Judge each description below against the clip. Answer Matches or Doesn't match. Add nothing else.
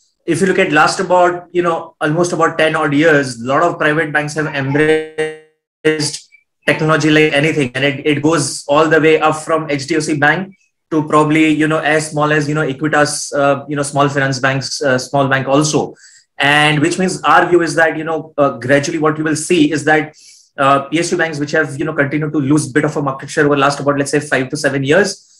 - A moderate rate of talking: Doesn't match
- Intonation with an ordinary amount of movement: Doesn't match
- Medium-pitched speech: Matches